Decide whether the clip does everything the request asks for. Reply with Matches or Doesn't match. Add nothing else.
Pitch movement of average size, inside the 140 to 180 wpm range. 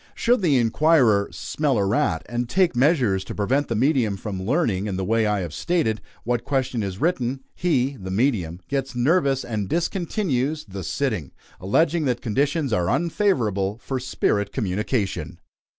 Doesn't match